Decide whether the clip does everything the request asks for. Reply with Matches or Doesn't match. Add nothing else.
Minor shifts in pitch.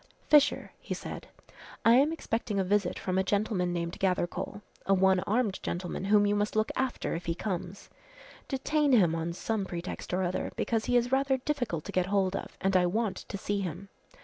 Doesn't match